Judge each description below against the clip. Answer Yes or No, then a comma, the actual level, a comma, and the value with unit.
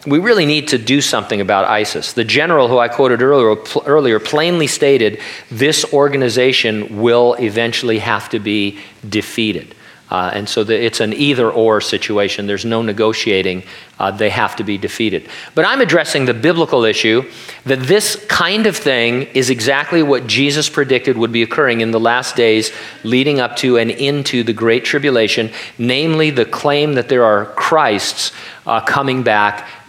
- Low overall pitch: Yes, low, 120 Hz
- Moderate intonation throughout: Yes, average, 4.4 semitones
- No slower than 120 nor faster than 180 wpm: Yes, average, 170 wpm